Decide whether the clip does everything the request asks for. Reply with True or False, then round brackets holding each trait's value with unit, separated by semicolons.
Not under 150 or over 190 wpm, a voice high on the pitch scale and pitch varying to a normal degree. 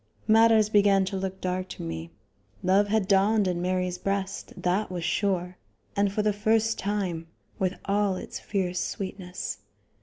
False (155 wpm; 195 Hz; 2.2 semitones)